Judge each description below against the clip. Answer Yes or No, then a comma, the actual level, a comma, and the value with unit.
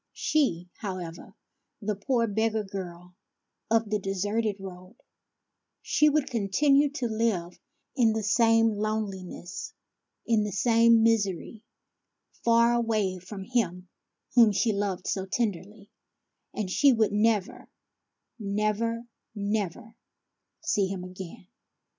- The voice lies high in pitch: Yes, high, 210 Hz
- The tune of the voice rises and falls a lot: No, average, 3.1 semitones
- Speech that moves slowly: Yes, slow, 115 wpm